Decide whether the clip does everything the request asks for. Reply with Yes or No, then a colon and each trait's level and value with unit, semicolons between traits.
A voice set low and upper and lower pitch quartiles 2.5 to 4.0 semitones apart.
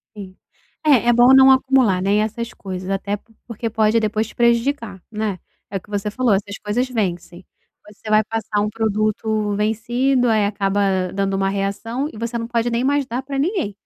No: high, 215 Hz; average, 3.0 semitones